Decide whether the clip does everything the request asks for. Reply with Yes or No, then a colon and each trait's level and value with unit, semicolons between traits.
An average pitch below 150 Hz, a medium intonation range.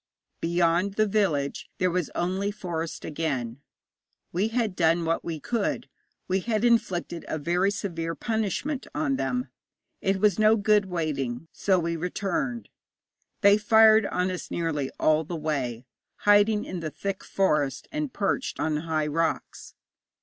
No: medium, 180 Hz; average, 4.6 semitones